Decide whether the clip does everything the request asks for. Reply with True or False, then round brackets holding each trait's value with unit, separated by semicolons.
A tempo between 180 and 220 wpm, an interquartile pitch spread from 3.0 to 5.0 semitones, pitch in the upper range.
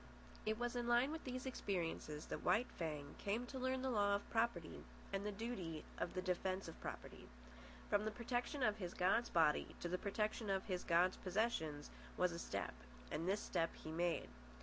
False (195 wpm; 5.4 semitones; 200 Hz)